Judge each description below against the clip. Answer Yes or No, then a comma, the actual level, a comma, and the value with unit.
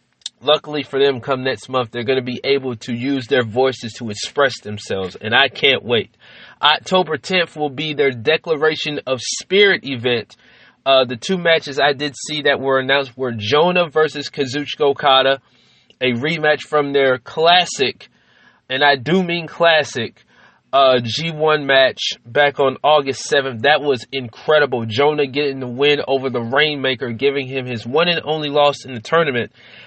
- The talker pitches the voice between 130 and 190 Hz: Yes, medium, 140 Hz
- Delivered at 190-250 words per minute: No, average, 165 wpm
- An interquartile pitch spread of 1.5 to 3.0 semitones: Yes, narrow, 2.5 semitones